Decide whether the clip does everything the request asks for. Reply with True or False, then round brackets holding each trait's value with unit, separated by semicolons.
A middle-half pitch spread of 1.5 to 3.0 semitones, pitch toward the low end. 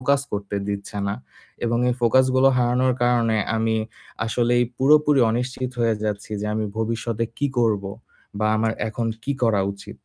True (2.5 semitones; 115 Hz)